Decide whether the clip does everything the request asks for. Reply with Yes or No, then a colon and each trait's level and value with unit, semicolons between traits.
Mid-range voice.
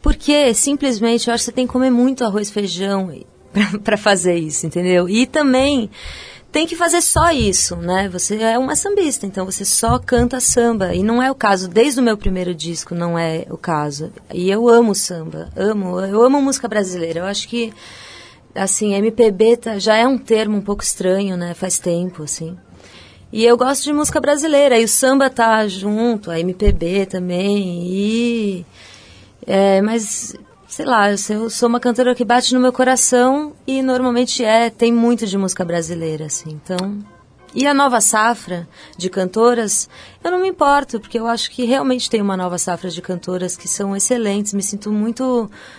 No: high, 215 Hz